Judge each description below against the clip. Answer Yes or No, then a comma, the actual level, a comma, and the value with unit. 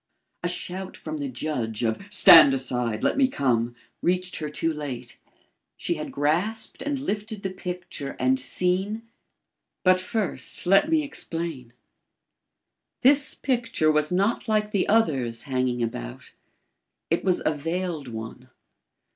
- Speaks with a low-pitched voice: No, medium, 165 Hz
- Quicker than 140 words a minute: No, slow, 135 wpm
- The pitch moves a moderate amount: No, wide, 7.3 semitones